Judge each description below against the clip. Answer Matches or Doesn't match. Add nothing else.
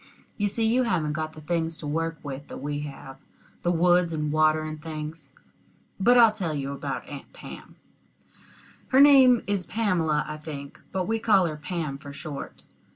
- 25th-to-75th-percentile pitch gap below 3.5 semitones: Doesn't match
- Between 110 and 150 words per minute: Doesn't match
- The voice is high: Doesn't match